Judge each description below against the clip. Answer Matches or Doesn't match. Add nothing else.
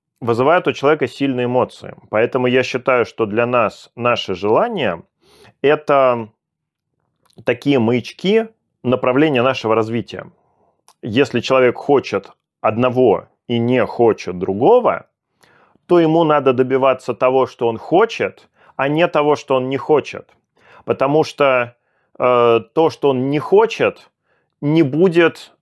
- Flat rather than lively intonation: Doesn't match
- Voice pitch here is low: Matches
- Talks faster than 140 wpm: Doesn't match